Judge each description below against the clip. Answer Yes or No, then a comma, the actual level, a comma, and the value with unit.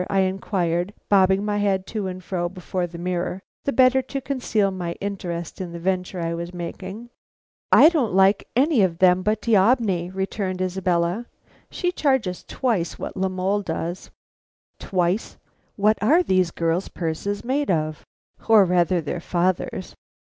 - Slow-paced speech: No, average, 155 wpm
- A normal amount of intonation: Yes, average, 3.1 semitones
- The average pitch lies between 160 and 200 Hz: Yes, high, 190 Hz